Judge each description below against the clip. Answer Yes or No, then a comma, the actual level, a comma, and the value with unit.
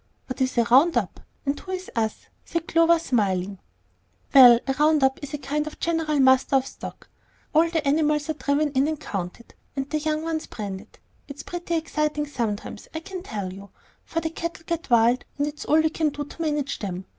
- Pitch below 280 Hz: No, very high, 290 Hz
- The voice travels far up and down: No, average, 4.3 semitones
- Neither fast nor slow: No, fast, 210 wpm